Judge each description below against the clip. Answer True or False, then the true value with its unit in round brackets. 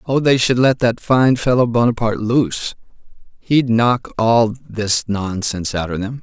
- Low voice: True (115 Hz)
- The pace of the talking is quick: False (155 wpm)